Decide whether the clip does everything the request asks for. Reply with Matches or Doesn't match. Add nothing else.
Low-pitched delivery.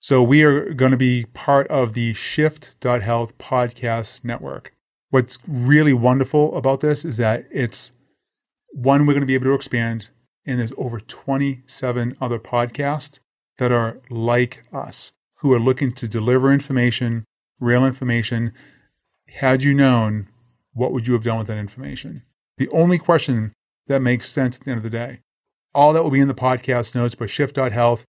Matches